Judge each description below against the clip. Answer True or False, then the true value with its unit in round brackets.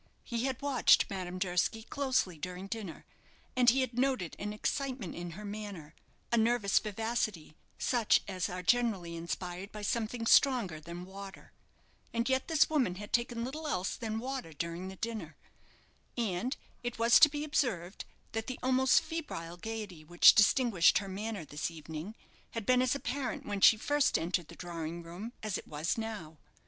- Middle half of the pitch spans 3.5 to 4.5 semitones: False (5.5 semitones)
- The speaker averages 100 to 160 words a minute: False (170 wpm)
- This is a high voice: True (210 Hz)